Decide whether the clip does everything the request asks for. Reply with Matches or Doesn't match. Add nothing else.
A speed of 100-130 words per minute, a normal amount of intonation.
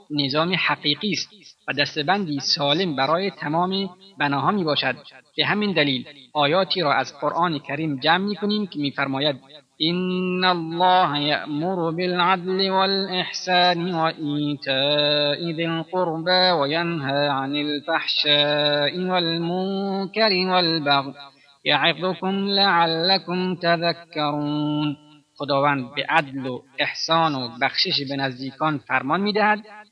Matches